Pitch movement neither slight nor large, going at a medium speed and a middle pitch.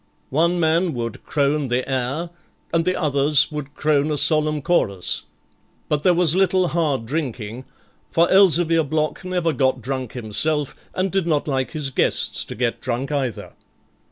Yes: average, 4.1 semitones; average, 155 wpm; medium, 150 Hz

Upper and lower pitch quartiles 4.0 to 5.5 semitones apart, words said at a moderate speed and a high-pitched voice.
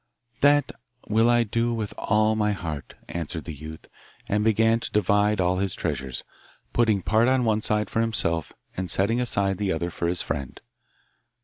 No: average, 4.3 semitones; average, 175 wpm; low, 105 Hz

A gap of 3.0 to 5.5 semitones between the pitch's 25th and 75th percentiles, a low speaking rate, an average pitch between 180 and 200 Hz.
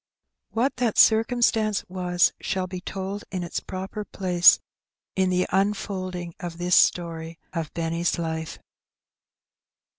No: narrow, 2.4 semitones; slow, 120 wpm; medium, 185 Hz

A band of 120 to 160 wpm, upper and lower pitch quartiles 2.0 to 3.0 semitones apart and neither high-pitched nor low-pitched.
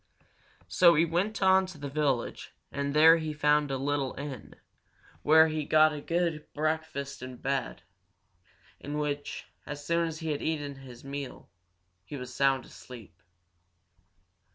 Yes: average, 155 wpm; narrow, 2.5 semitones; medium, 150 Hz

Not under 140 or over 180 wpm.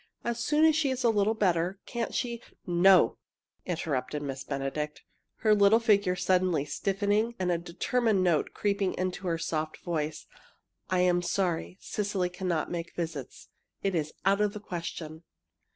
Yes: average, 160 wpm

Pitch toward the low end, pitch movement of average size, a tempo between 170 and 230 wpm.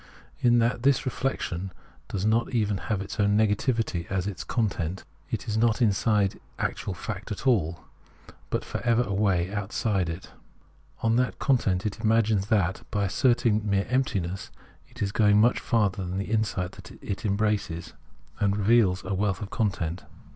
No: low, 105 Hz; average, 3.0 semitones; average, 160 wpm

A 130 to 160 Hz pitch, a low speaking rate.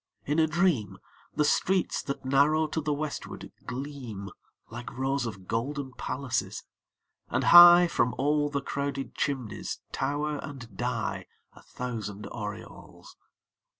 Yes: medium, 140 Hz; slow, 125 wpm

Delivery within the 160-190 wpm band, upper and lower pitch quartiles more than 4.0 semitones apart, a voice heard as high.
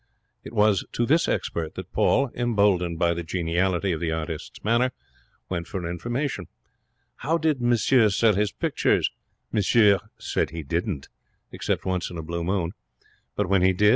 No: average, 165 wpm; average, 5.2 semitones; very low, 95 Hz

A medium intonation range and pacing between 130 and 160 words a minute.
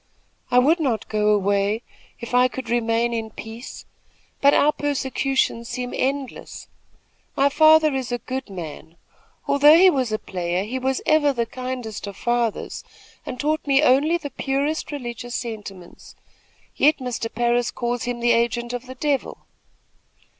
Yes: average, 3.3 semitones; average, 155 wpm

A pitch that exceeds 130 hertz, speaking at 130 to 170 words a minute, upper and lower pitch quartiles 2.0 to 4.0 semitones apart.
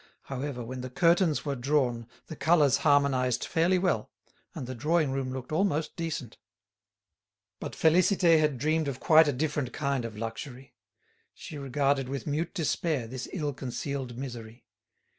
Yes: medium, 140 Hz; average, 150 wpm; average, 3.7 semitones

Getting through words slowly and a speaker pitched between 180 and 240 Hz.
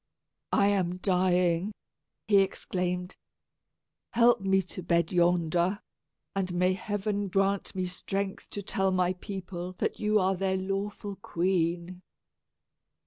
Yes: slow, 125 wpm; medium, 185 Hz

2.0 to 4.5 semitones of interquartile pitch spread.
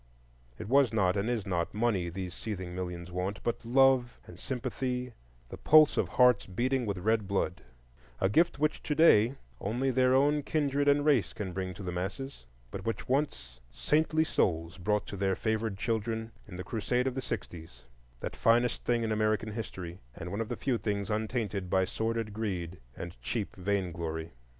No: average, 5.2 semitones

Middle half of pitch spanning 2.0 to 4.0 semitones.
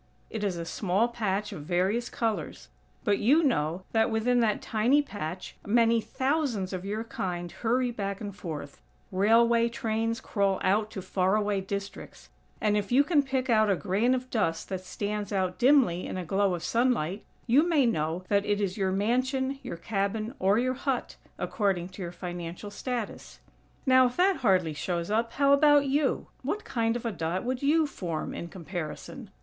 No: average, 4.8 semitones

